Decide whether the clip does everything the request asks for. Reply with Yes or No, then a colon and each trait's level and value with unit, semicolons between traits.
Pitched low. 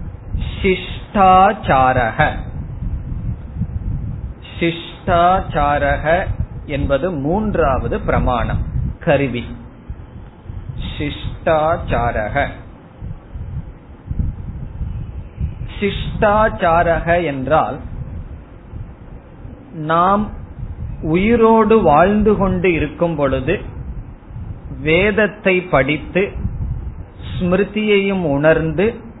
No: medium, 160 Hz